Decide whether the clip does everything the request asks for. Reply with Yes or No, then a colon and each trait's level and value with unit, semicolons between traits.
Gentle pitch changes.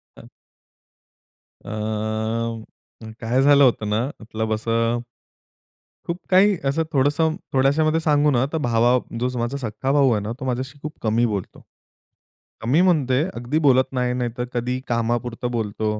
No: average, 3.7 semitones